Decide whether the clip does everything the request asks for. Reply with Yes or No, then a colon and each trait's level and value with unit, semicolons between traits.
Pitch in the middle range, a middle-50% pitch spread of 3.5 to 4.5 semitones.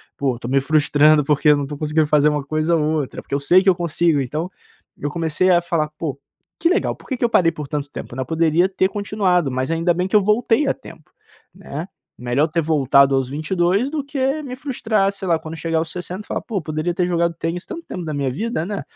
Yes: medium, 165 Hz; average, 4.2 semitones